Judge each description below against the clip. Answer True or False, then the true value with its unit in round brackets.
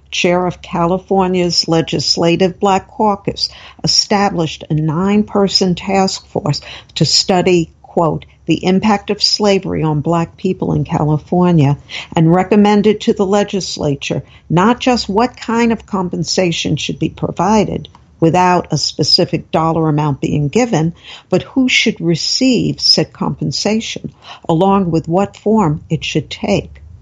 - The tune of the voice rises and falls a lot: False (3.8 semitones)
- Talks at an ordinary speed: False (125 wpm)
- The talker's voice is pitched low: False (180 Hz)